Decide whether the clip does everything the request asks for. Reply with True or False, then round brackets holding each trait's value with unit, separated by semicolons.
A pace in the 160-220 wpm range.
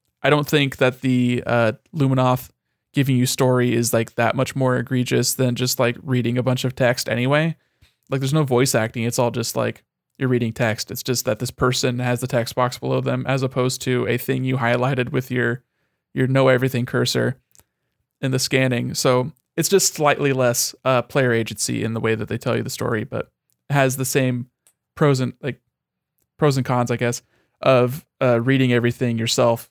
True (200 wpm)